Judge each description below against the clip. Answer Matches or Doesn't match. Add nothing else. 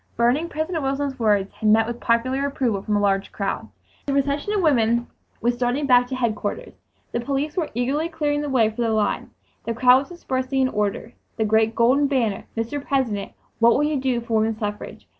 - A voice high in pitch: Matches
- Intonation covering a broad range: Doesn't match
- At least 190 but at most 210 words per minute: Matches